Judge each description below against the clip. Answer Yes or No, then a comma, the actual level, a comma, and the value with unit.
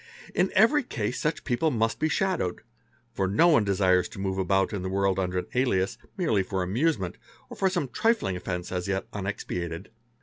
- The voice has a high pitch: No, low, 100 Hz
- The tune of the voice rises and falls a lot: Yes, wide, 8.0 semitones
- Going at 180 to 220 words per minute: Yes, average, 190 wpm